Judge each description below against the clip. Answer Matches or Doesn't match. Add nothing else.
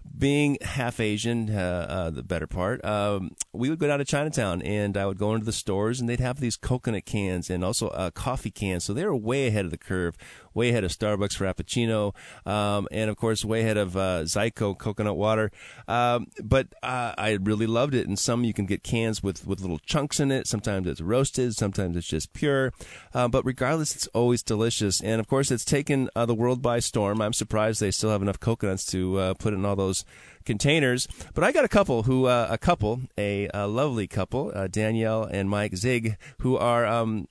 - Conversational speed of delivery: Doesn't match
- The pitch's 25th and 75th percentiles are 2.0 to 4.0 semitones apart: Matches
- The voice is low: Matches